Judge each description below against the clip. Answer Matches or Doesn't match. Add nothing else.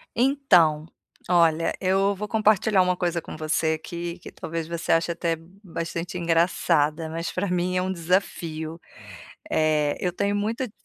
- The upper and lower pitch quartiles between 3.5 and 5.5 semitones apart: Doesn't match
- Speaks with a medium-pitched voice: Matches